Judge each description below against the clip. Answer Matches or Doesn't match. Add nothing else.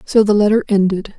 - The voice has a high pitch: Matches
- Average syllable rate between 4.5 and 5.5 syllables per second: Doesn't match